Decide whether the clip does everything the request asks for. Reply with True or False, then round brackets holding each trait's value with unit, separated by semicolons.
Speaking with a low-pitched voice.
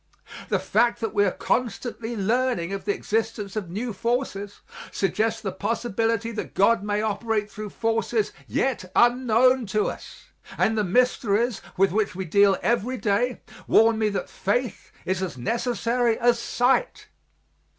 False (225 Hz)